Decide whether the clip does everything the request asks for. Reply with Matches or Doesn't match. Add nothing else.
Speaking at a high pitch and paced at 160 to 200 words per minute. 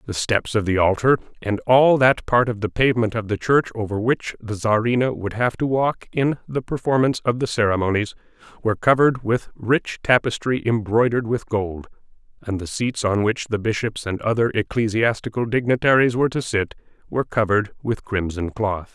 Doesn't match